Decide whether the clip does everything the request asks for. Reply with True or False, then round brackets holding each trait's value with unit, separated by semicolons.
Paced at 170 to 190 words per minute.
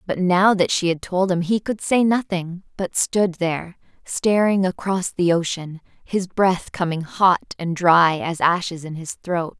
True (180 wpm)